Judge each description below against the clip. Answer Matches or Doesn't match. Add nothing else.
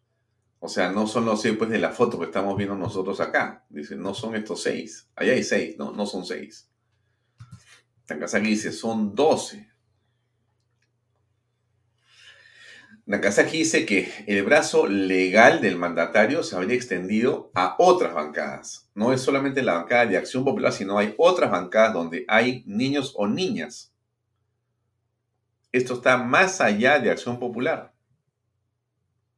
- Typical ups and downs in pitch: Doesn't match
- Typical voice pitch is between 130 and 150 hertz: Doesn't match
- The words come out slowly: Doesn't match